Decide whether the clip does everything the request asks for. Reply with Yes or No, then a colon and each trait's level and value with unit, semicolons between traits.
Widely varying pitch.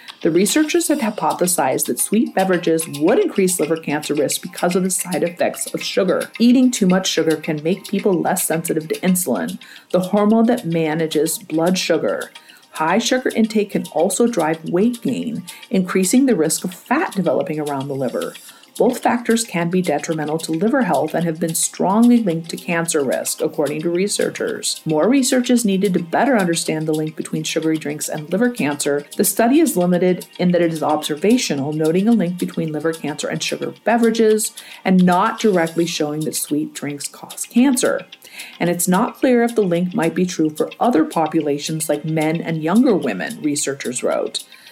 Yes: wide, 5.9 semitones